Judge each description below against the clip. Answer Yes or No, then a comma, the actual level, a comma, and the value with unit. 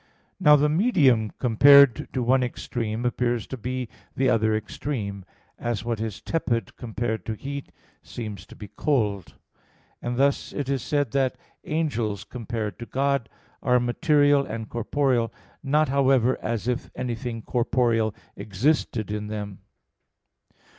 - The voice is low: Yes, low, 120 Hz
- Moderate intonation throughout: Yes, average, 3.9 semitones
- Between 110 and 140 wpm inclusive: Yes, slow, 135 wpm